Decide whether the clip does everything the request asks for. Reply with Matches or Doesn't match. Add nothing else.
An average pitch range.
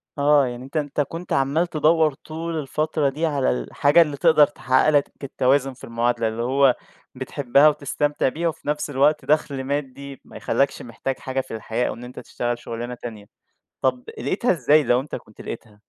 Matches